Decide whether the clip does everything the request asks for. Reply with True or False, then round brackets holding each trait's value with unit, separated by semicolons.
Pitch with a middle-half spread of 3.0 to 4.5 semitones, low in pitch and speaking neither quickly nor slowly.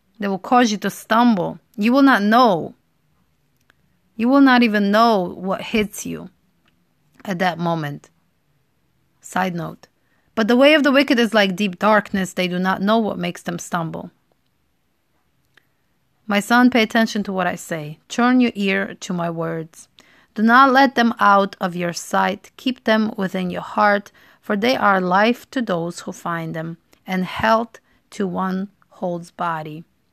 False (4.2 semitones; 200 Hz; 165 wpm)